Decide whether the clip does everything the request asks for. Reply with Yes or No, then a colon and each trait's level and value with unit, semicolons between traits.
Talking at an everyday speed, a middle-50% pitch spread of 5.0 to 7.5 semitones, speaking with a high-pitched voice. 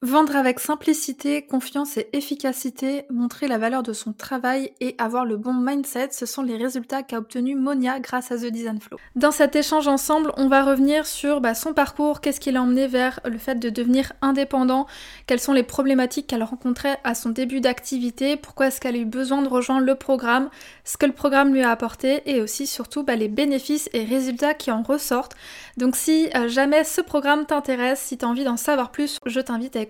No: average, 205 wpm; narrow, 2.4 semitones; very high, 265 Hz